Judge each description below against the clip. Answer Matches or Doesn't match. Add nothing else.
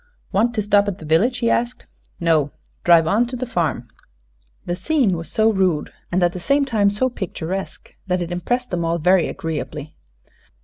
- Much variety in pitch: Matches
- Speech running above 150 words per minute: Matches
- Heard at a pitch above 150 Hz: Matches